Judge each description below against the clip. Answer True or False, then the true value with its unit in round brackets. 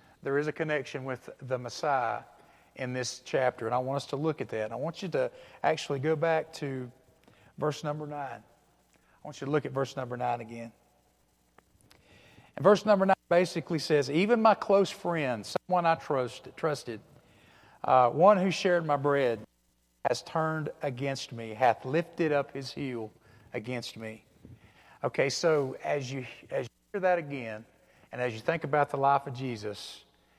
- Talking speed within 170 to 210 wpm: True (180 wpm)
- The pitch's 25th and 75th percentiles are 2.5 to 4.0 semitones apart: False (4.8 semitones)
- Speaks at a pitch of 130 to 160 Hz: True (140 Hz)